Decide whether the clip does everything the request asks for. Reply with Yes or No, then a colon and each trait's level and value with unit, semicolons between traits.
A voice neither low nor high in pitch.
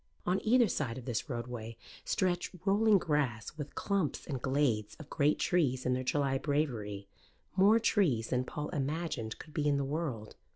Yes: medium, 145 Hz